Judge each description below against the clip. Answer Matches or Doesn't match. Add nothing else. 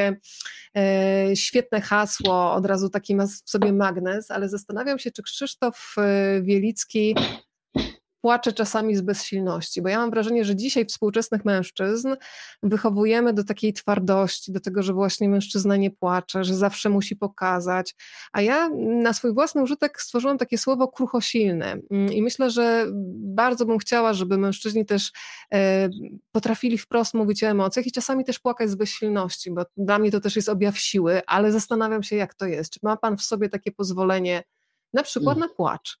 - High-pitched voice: Matches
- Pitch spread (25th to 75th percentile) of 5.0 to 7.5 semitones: Doesn't match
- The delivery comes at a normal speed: Doesn't match